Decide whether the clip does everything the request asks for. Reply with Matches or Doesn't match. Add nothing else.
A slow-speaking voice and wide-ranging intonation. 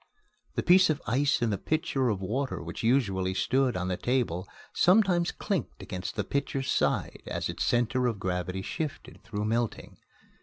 Doesn't match